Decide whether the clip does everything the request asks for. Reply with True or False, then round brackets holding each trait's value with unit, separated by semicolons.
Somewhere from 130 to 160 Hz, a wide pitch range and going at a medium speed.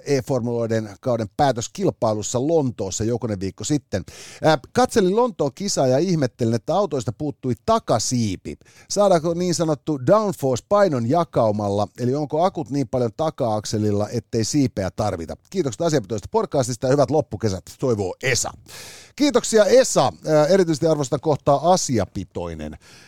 True (135 Hz; 6.7 semitones; 115 wpm)